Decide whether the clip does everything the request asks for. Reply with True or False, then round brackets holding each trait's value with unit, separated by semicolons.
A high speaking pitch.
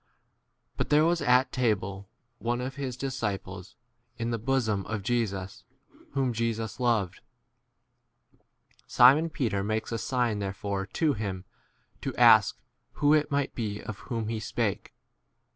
False (115 Hz)